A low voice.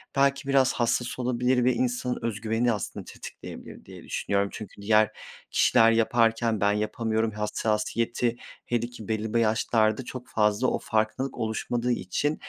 Yes: low, 115 Hz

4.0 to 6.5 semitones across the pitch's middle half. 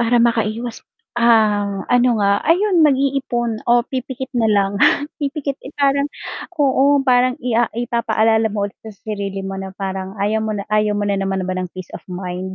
Yes: average, 4.4 semitones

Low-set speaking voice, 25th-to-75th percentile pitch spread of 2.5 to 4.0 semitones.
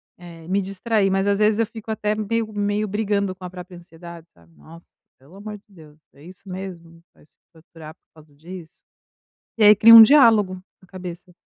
No: high, 190 Hz; average, 3.7 semitones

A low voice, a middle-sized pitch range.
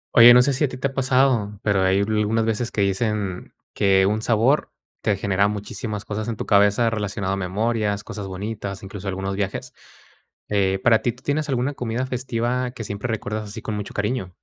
Yes: low, 105 Hz; average, 3.1 semitones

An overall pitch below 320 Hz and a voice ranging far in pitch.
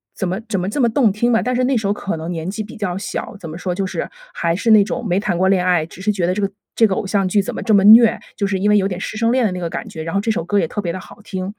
No: high, 195 Hz; average, 3.0 semitones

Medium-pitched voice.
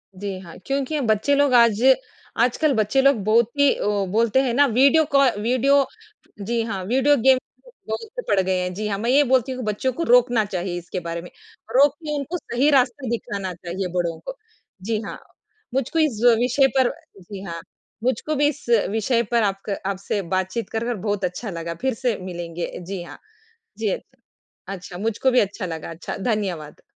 No: high, 225 Hz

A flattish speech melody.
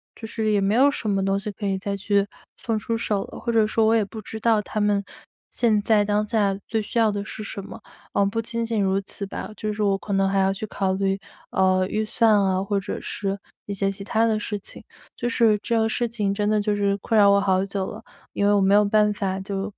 Yes: narrow, 1.8 semitones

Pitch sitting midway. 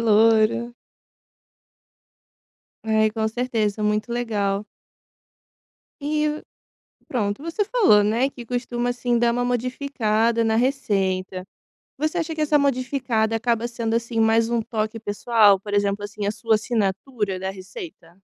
No: high, 230 Hz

